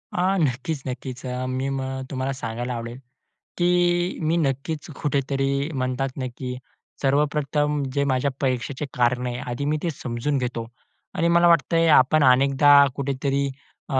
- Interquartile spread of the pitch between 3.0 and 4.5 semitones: No, narrow, 2.6 semitones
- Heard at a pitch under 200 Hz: Yes, low, 135 Hz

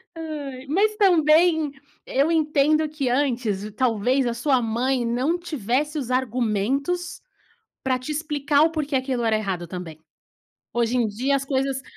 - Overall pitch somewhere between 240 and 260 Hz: No, very high, 270 Hz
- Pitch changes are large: No, average, 4.2 semitones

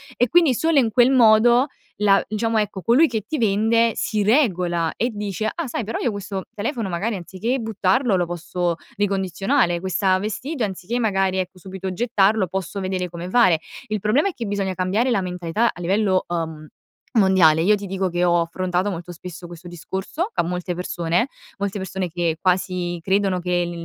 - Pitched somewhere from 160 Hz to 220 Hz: Yes, high, 190 Hz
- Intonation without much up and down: No, average, 3.8 semitones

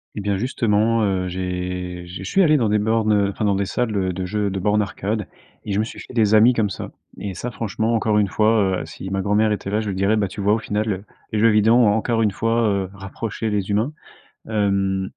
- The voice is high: No, low, 105 Hz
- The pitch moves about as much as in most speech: No, narrow, 2.3 semitones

